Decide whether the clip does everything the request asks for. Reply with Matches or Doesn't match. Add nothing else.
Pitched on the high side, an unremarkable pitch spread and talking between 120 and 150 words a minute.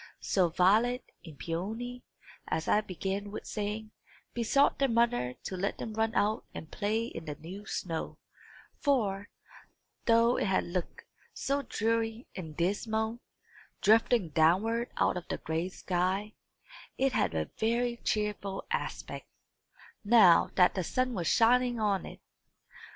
Matches